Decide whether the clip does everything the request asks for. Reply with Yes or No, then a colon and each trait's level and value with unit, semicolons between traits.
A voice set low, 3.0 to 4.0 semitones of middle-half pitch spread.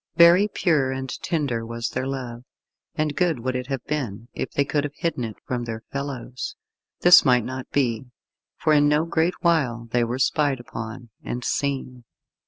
Yes: low, 130 Hz; average, 3.7 semitones